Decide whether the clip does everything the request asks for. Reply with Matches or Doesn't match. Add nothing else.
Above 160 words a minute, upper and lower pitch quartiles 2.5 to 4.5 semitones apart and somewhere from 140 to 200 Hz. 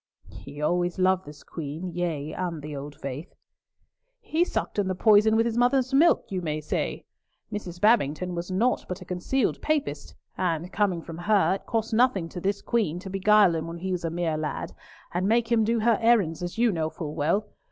Doesn't match